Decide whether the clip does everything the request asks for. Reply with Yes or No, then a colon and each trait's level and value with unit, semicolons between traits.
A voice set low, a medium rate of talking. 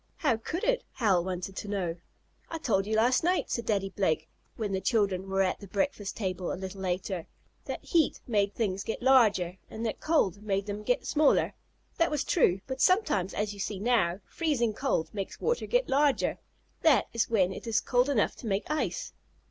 No: high, 210 Hz; average, 195 wpm